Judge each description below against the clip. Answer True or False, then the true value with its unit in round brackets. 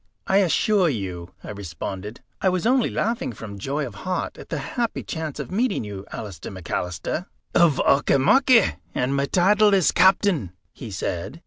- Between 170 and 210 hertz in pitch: False (140 Hz)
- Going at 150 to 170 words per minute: True (160 wpm)